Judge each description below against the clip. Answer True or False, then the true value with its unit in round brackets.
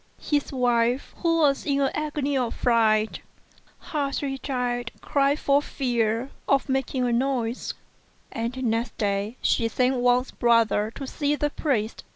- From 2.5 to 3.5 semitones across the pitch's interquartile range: True (3.1 semitones)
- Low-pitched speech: False (250 Hz)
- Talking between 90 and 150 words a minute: True (145 wpm)